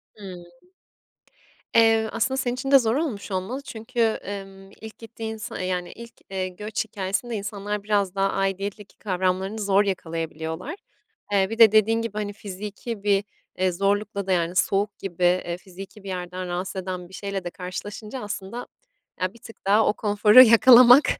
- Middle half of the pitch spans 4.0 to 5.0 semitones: No, average, 3.0 semitones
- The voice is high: Yes, high, 200 Hz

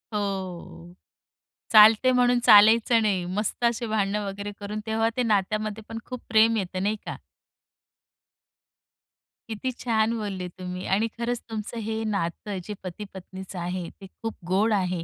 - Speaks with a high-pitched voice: Yes, high, 210 Hz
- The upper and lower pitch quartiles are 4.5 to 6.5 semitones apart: No, average, 2.8 semitones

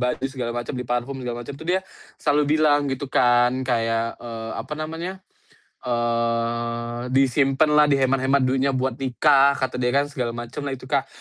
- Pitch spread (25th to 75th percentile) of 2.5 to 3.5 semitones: Yes, average, 2.9 semitones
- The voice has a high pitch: No, low, 130 Hz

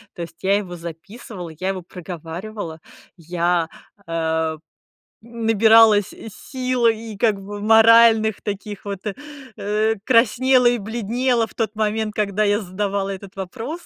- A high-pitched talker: Yes, high, 210 Hz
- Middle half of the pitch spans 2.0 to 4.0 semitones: Yes, average, 3.4 semitones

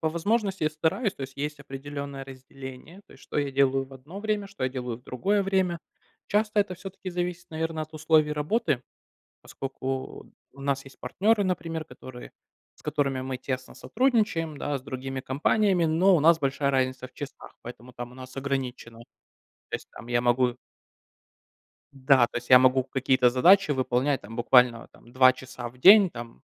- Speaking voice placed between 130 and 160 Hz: Yes, medium, 140 Hz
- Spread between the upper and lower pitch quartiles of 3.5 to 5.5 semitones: Yes, average, 4.7 semitones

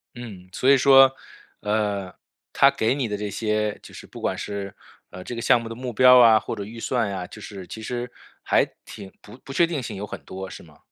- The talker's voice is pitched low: Yes, low, 110 Hz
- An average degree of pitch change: Yes, average, 3.7 semitones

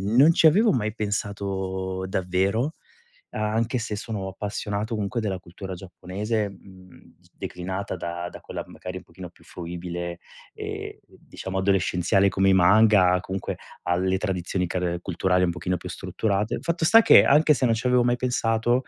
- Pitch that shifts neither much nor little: Yes, average, 3.6 semitones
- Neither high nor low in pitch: No, very low, 95 Hz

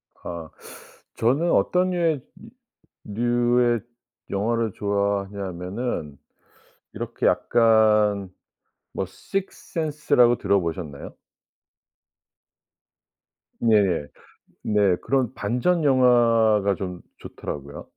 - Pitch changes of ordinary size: Yes, average, 4.0 semitones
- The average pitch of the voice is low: Yes, low, 110 Hz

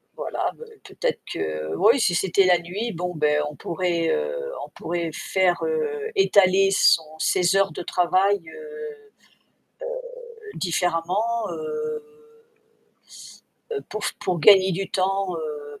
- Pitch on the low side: No, high, 190 Hz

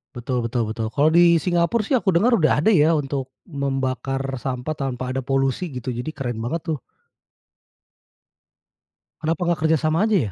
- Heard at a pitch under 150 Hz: Yes, medium, 140 Hz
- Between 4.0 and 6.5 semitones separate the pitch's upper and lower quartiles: Yes, average, 4.4 semitones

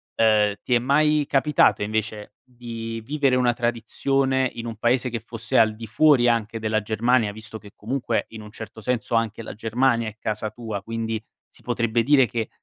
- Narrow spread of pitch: Yes, narrow, 2.3 semitones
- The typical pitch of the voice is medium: No, low, 115 Hz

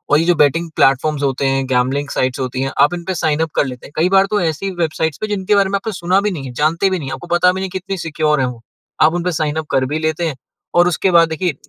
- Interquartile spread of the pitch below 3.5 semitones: No, average, 4.5 semitones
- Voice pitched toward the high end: No, medium, 160 Hz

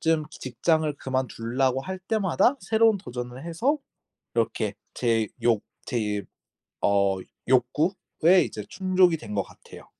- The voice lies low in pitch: Yes, low, 130 Hz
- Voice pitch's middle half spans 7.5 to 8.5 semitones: Yes, wide, 7.9 semitones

